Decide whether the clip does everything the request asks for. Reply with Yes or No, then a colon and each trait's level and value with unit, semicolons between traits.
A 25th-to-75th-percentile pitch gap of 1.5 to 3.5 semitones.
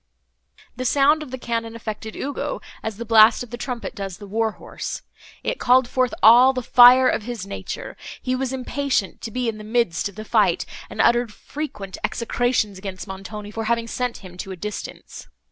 Yes: average, 3.2 semitones